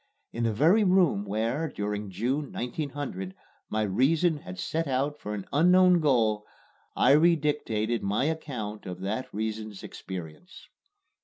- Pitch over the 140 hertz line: No, low, 120 Hz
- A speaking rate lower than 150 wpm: Yes, slow, 135 wpm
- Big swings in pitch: Yes, wide, 6.5 semitones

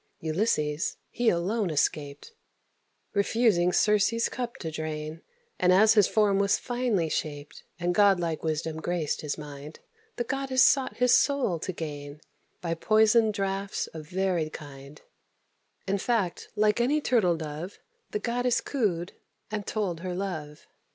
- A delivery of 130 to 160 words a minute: Yes, average, 140 wpm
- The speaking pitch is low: No, medium, 185 Hz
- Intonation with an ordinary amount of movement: No, wide, 5.8 semitones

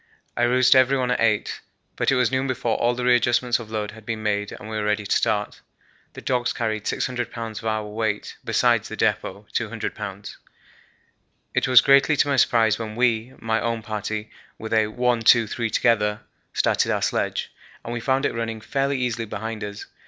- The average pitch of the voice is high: No, low, 115 Hz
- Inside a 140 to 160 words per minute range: No, average, 195 wpm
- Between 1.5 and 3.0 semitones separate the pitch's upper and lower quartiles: Yes, narrow, 2.4 semitones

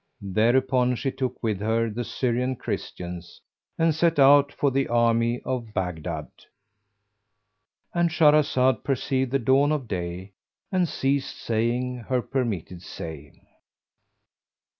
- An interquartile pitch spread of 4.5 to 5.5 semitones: No, average, 3.9 semitones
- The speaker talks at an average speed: No, slow, 120 wpm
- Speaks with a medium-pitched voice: No, low, 125 Hz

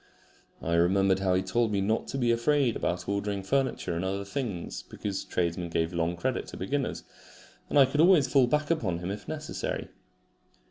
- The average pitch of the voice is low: Yes, low, 100 Hz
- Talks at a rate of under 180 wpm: No, average, 190 wpm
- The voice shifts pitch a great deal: Yes, wide, 6.6 semitones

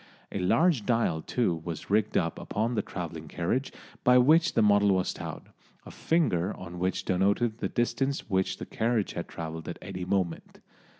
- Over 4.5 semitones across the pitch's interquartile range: Yes, average, 5.2 semitones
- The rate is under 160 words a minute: No, average, 175 wpm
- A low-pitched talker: Yes, low, 100 Hz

